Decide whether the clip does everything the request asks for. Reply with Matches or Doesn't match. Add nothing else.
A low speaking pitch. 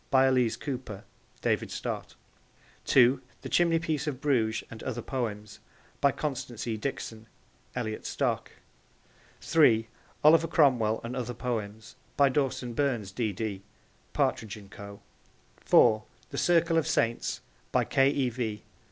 Matches